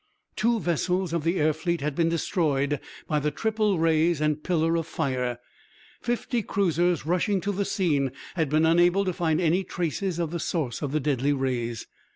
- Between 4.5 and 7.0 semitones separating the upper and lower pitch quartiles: No, average, 3.3 semitones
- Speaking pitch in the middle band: Yes, medium, 165 Hz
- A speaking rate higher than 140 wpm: Yes, average, 185 wpm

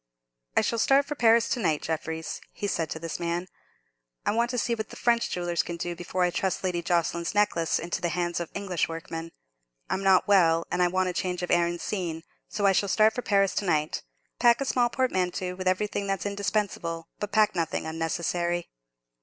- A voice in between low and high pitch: Yes, medium, 180 Hz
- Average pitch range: Yes, average, 3.4 semitones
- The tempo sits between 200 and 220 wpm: Yes, fast, 205 wpm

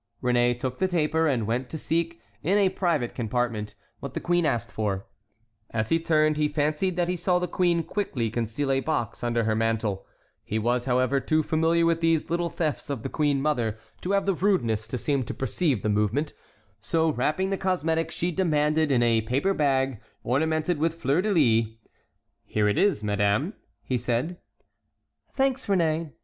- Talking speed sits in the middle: Yes, average, 180 wpm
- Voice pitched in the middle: Yes, medium, 145 Hz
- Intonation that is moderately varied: No, wide, 5.9 semitones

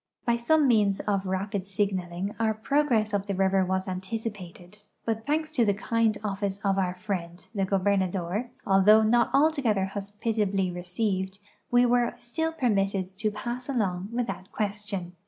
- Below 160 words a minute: Yes, average, 150 wpm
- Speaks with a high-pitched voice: Yes, high, 205 Hz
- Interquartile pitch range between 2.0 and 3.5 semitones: Yes, average, 3.2 semitones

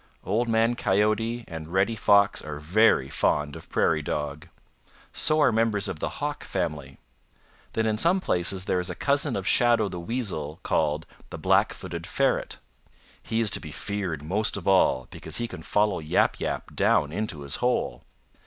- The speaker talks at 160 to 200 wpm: Yes, average, 175 wpm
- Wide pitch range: Yes, wide, 6.2 semitones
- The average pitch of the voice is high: No, very low, 95 Hz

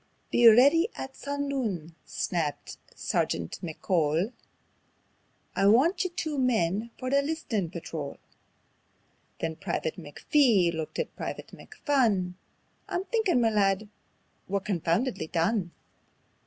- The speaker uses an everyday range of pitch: No, wide, 8.5 semitones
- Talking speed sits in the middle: No, slow, 110 wpm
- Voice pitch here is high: Yes, high, 215 Hz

